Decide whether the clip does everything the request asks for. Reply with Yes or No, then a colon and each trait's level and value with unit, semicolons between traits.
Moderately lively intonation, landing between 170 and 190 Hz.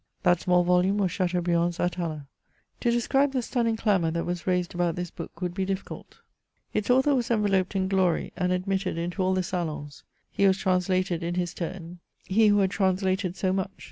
No: narrow, 1.9 semitones; medium, 185 Hz